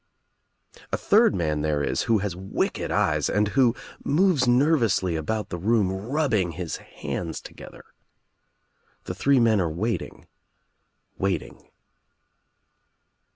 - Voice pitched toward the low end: Yes, low, 100 Hz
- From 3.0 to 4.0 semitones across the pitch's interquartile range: No, average, 5.3 semitones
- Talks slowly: Yes, slow, 120 wpm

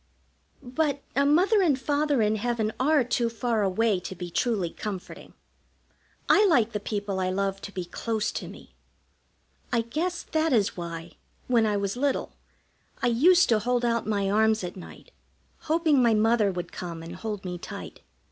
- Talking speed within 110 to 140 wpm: No, average, 175 wpm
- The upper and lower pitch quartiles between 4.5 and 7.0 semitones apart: Yes, average, 4.9 semitones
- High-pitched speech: Yes, high, 225 Hz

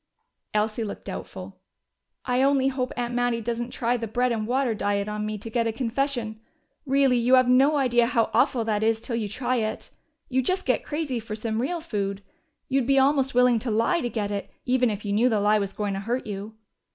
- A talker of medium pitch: No, high, 235 Hz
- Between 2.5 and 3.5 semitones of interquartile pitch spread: Yes, average, 3.1 semitones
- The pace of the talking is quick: Yes, fast, 220 wpm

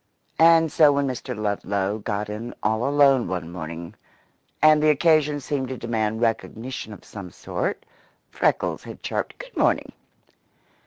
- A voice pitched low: Yes, low, 120 Hz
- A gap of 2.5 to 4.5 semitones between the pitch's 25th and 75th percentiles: No, wide, 5.6 semitones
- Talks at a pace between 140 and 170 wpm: Yes, average, 145 wpm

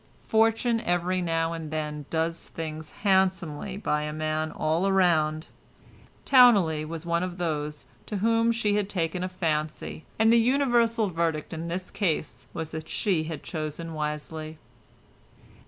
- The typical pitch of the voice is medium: Yes, medium, 170 Hz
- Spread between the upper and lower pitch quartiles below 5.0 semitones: Yes, average, 4.0 semitones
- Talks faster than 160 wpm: No, average, 145 wpm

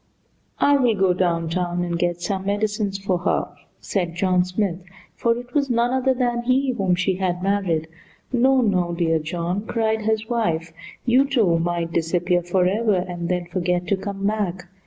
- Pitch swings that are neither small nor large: Yes, average, 4.1 semitones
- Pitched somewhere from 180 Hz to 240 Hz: Yes, high, 190 Hz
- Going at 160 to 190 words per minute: Yes, average, 170 wpm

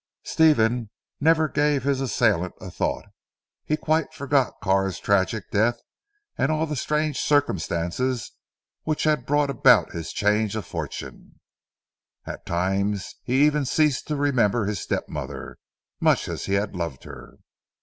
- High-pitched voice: No, low, 125 Hz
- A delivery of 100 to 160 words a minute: Yes, average, 140 wpm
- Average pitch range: No, wide, 6.6 semitones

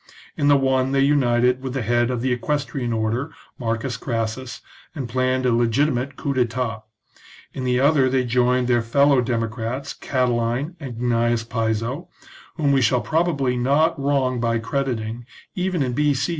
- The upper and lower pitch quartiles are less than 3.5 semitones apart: Yes, average, 2.7 semitones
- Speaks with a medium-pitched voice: No, low, 125 Hz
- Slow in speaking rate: No, average, 155 wpm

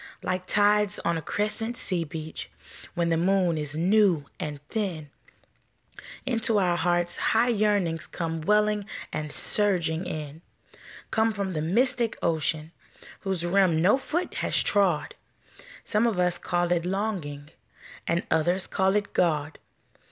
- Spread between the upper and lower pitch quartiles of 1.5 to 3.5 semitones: No, average, 4.3 semitones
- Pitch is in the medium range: Yes, medium, 180 Hz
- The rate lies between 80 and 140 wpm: Yes, slow, 135 wpm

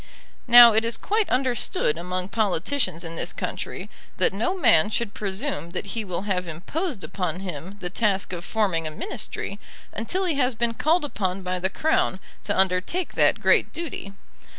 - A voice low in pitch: No, high, 200 Hz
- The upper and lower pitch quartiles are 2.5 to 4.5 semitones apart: No, average, 5.1 semitones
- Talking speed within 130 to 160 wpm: No, average, 175 wpm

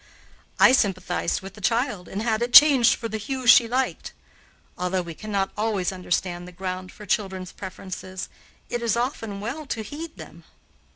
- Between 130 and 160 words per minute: No, average, 170 wpm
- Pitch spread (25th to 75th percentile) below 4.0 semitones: No, average, 4.3 semitones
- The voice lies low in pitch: No, high, 210 Hz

